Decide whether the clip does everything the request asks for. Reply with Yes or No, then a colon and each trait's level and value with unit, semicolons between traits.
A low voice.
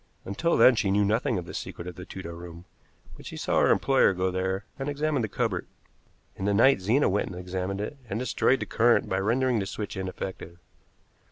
Yes: low, 100 Hz